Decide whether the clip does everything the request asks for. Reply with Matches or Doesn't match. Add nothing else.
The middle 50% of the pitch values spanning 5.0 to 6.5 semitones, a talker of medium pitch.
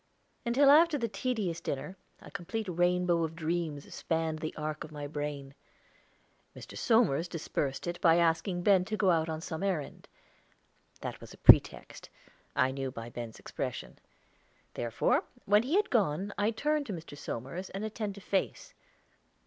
Matches